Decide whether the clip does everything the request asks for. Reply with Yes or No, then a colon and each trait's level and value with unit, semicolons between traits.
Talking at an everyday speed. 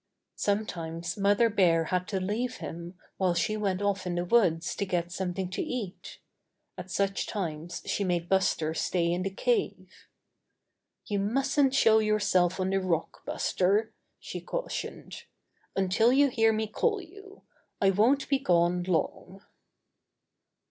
Yes: average, 150 wpm